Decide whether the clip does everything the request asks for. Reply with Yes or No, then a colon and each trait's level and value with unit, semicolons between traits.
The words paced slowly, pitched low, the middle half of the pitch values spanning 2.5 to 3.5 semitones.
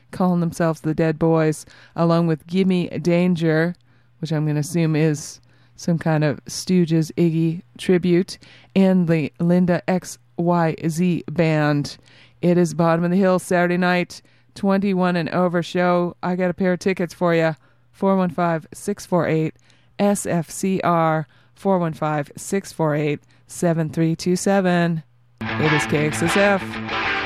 No: slow, 120 wpm; medium, 165 Hz; average, 2.9 semitones